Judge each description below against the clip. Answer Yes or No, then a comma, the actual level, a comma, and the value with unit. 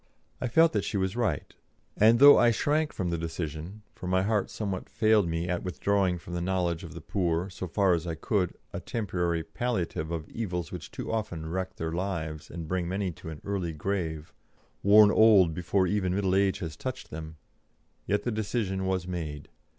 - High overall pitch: No, very low, 95 Hz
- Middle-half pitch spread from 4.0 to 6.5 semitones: No, average, 3.5 semitones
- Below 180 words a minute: No, average, 195 wpm